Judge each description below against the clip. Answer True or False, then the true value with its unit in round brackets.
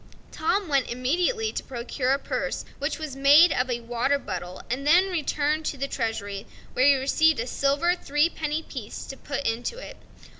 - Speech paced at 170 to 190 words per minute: True (185 wpm)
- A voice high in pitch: True (280 Hz)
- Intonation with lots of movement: False (4.1 semitones)